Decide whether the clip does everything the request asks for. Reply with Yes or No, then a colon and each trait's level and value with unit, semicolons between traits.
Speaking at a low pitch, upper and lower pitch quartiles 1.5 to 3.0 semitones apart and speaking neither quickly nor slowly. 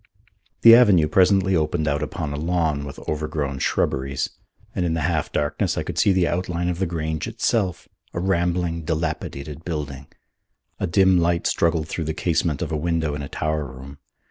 Yes: very low, 80 Hz; average, 2.7 semitones; average, 180 wpm